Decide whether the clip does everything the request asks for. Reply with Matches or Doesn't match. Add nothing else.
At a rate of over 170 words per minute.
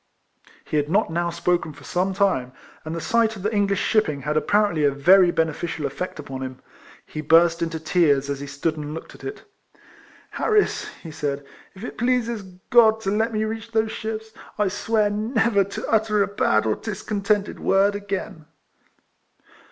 Matches